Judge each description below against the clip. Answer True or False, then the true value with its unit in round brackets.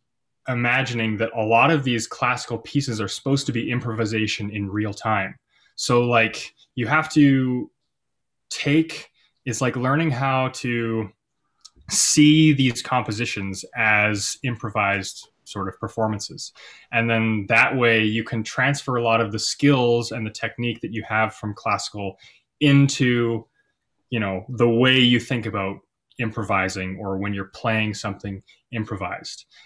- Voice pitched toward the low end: True (115 Hz)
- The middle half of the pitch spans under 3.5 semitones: True (2.9 semitones)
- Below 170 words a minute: True (140 wpm)